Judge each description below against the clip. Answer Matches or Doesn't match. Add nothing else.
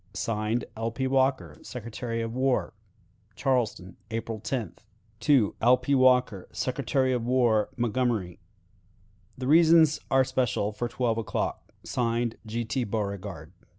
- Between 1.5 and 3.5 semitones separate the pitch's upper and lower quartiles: Matches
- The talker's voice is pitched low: Matches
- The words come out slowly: Matches